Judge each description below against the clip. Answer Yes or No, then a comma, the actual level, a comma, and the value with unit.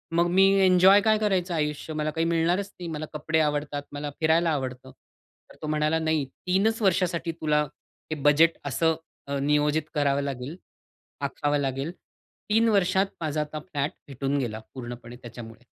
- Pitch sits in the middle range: Yes, medium, 150 Hz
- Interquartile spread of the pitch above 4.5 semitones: No, average, 3.2 semitones